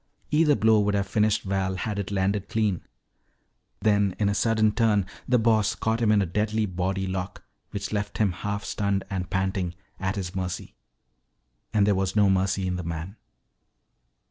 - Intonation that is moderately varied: No, narrow, 2.0 semitones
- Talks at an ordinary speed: Yes, average, 175 wpm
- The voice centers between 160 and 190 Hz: No, low, 100 Hz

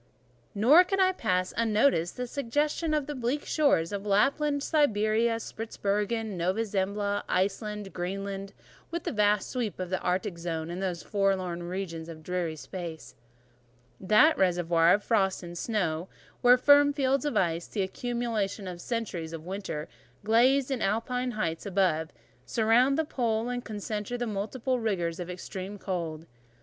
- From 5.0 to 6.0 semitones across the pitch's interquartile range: Yes, average, 5.3 semitones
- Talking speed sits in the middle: Yes, average, 150 wpm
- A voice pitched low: No, high, 205 Hz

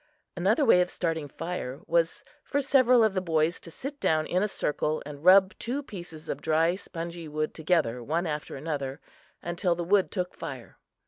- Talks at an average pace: Yes, average, 185 wpm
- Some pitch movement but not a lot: Yes, average, 3.5 semitones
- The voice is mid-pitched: Yes, medium, 170 Hz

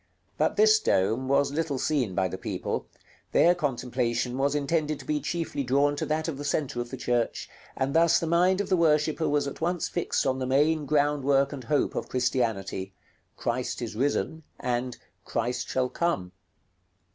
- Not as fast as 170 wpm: No, average, 180 wpm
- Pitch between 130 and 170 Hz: Yes, medium, 140 Hz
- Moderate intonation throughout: Yes, average, 3.9 semitones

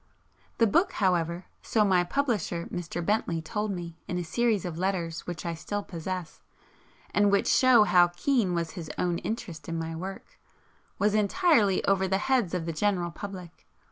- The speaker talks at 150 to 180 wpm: Yes, average, 175 wpm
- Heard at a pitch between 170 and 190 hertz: Yes, medium, 185 Hz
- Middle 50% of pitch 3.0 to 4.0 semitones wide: Yes, average, 3.5 semitones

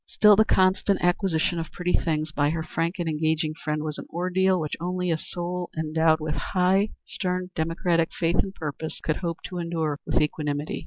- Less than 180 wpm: No, average, 190 wpm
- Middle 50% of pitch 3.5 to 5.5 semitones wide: No, narrow, 2.5 semitones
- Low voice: No, medium, 165 Hz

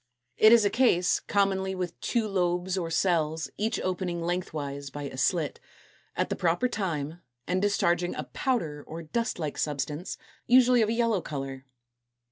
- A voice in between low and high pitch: Yes, medium, 175 Hz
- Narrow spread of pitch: No, average, 4.6 semitones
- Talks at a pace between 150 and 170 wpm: Yes, average, 160 wpm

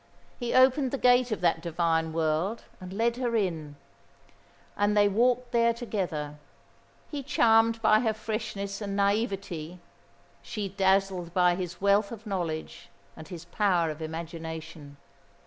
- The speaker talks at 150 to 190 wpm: No, average, 140 wpm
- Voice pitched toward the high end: Yes, high, 195 Hz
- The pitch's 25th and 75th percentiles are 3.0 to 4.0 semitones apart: No, average, 5.2 semitones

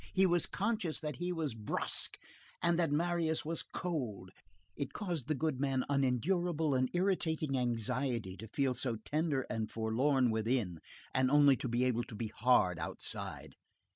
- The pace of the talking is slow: No, average, 155 wpm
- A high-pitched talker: No, low, 135 Hz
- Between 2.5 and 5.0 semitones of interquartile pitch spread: No, wide, 5.4 semitones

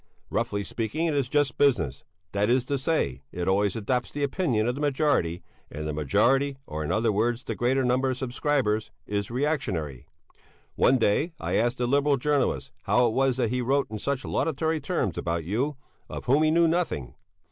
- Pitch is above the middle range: No, low, 125 Hz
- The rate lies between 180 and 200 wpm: Yes, average, 190 wpm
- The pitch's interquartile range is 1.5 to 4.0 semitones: No, wide, 5.4 semitones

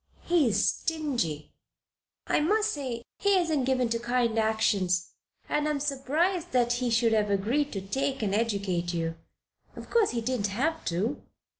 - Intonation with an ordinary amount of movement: No, wide, 6.2 semitones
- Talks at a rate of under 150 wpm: No, average, 175 wpm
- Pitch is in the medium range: No, high, 240 Hz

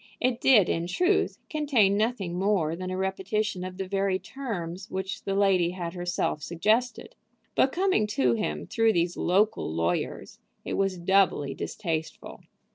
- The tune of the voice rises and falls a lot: No, average, 3.8 semitones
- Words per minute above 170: No, average, 150 wpm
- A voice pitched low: No, high, 190 Hz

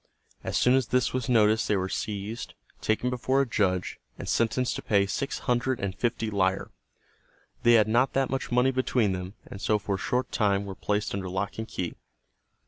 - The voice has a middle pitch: No, low, 110 Hz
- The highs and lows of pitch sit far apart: No, average, 3.9 semitones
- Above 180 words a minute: Yes, average, 200 wpm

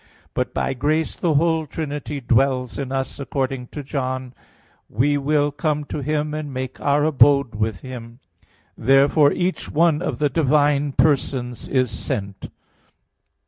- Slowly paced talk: No, average, 145 wpm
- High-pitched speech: No, medium, 140 Hz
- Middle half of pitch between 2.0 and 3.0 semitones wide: Yes, narrow, 2.5 semitones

